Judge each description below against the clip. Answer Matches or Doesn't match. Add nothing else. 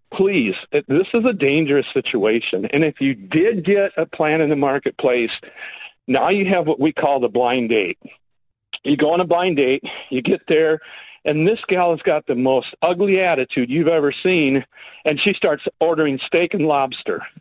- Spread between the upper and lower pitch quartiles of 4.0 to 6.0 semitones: Matches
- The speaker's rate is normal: Matches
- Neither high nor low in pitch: Matches